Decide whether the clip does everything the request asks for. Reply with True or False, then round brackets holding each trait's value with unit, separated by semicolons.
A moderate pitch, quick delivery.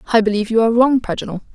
False (225 Hz; 230 wpm)